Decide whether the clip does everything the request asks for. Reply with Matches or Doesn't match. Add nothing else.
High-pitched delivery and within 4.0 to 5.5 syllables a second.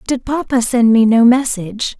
Matches